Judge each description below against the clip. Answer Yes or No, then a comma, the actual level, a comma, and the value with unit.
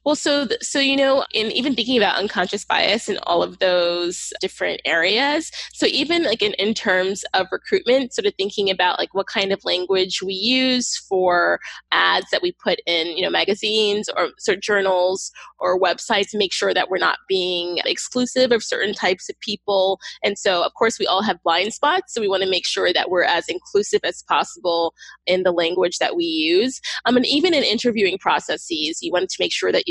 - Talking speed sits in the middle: No, fast, 210 wpm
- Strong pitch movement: Yes, wide, 7.0 semitones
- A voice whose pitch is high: Yes, high, 210 Hz